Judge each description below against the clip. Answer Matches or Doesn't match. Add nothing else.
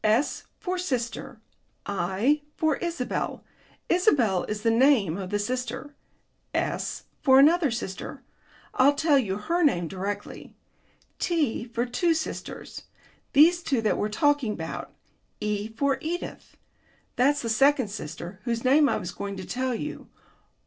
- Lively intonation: Matches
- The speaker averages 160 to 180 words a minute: Doesn't match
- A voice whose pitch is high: Matches